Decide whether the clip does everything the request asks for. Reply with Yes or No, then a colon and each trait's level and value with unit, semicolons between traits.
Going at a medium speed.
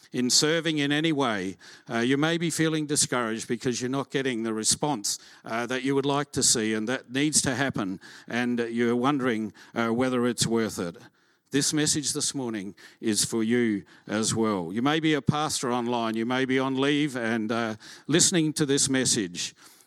Yes: average, 190 wpm